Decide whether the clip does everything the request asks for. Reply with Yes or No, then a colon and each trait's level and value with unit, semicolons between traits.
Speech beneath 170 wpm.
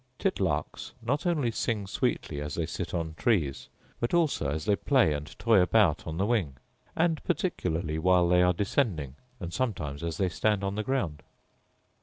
No: average, 175 wpm